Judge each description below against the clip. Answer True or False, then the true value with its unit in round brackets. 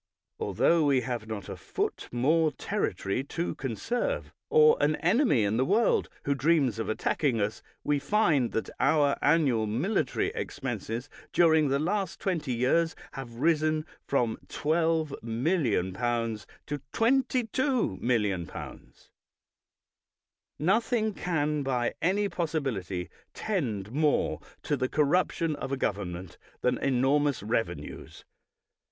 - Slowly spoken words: True (115 wpm)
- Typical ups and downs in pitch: False (6.1 semitones)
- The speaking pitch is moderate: True (145 Hz)